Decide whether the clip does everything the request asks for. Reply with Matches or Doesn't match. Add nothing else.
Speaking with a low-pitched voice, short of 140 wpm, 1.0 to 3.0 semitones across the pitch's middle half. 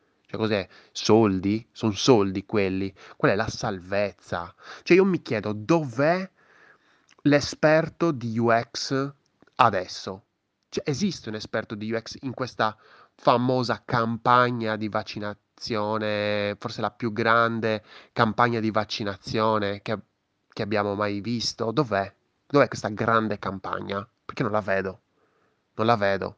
Matches